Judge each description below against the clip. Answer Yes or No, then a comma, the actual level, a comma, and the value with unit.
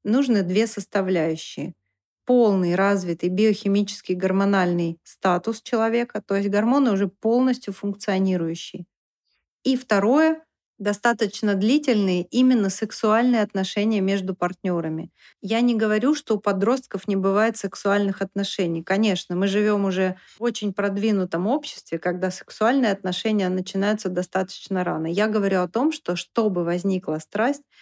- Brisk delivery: No, average, 120 wpm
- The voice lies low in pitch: No, high, 200 Hz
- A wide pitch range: No, average, 3.0 semitones